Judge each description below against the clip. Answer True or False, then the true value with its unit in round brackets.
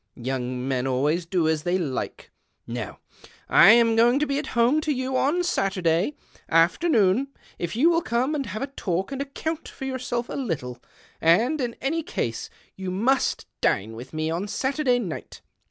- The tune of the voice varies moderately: False (8.8 semitones)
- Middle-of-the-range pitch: False (225 Hz)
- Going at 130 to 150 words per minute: False (175 wpm)